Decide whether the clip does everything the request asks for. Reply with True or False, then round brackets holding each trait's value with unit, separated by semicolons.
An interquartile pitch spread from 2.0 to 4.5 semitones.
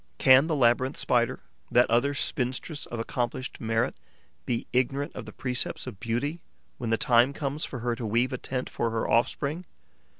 True (2.7 semitones)